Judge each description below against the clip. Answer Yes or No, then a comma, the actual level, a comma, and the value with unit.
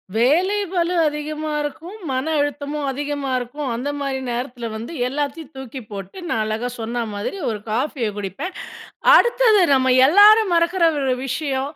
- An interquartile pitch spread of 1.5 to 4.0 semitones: No, average, 4.7 semitones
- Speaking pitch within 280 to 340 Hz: Yes, very high, 285 Hz